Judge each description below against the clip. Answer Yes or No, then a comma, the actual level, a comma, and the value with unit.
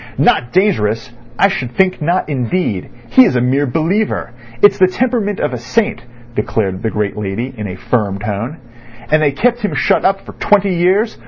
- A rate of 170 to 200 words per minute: Yes, average, 180 wpm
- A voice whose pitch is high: No, medium, 140 Hz